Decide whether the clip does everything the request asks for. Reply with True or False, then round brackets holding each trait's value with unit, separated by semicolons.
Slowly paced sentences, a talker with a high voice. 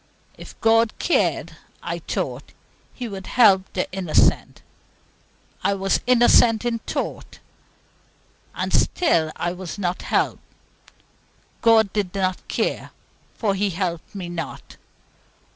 True (115 wpm; 195 Hz)